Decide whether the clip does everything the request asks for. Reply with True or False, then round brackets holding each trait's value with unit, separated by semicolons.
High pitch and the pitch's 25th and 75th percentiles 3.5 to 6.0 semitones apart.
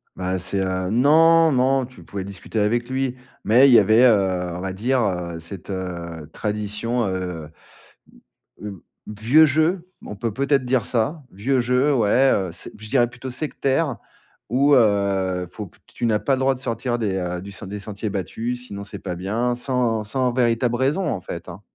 False (115 Hz; 5.0 semitones)